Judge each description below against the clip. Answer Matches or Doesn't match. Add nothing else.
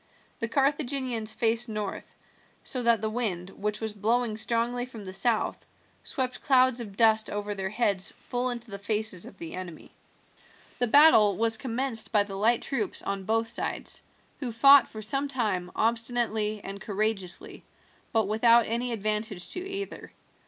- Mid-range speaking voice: Doesn't match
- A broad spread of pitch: Doesn't match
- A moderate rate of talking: Matches